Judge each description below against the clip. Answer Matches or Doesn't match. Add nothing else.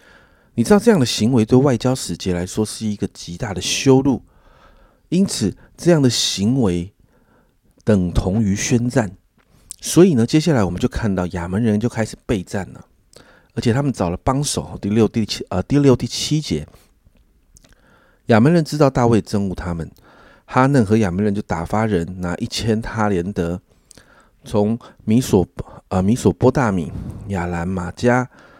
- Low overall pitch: Matches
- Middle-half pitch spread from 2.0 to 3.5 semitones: Doesn't match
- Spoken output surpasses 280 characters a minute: Doesn't match